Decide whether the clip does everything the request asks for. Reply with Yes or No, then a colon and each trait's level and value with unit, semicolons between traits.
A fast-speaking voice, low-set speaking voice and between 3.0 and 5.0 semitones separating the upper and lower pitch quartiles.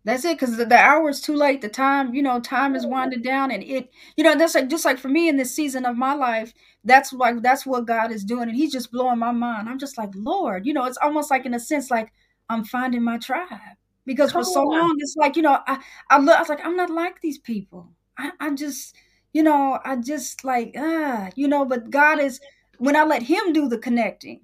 No: fast, 255 wpm; very high, 270 Hz; average, 3.4 semitones